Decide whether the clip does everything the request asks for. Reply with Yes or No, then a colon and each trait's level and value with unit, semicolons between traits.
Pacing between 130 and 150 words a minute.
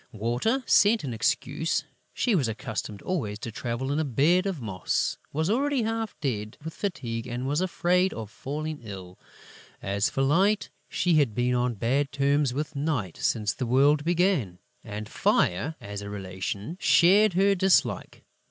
No: average, 160 wpm